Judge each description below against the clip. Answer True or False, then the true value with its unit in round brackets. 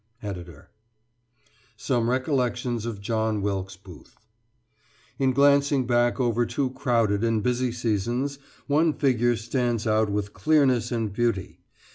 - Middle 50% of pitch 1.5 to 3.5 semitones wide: True (3.1 semitones)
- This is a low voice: True (120 Hz)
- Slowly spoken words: True (120 wpm)